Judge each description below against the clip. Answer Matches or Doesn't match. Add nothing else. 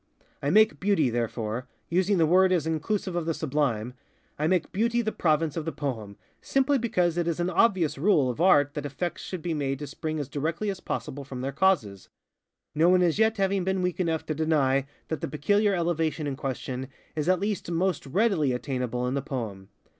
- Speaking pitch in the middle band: Matches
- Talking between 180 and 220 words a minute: Matches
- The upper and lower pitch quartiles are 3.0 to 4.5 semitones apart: Doesn't match